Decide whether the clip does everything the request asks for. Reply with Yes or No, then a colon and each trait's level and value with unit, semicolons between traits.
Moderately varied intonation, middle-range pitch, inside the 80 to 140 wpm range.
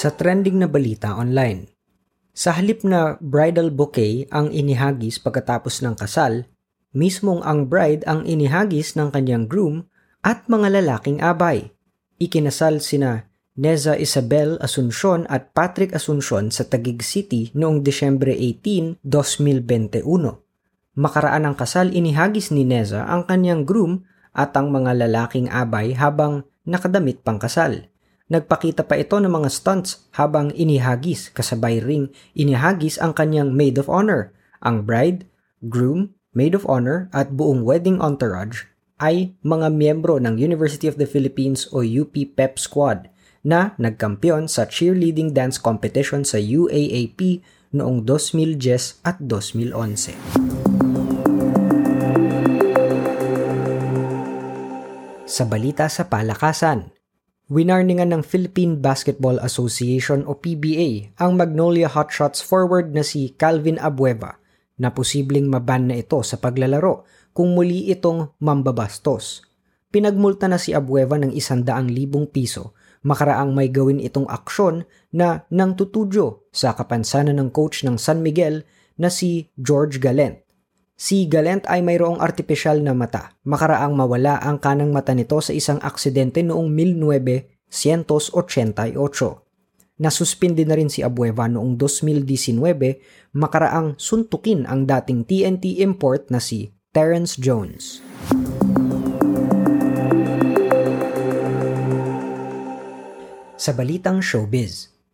Yes: average, 5.0 semitones; medium, 145 Hz; average, 120 wpm